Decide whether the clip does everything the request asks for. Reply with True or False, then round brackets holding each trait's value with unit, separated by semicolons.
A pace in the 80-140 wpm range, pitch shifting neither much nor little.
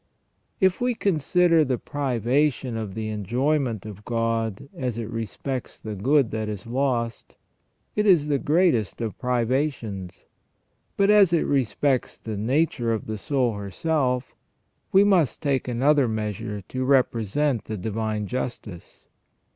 True (135 wpm; 4.9 semitones)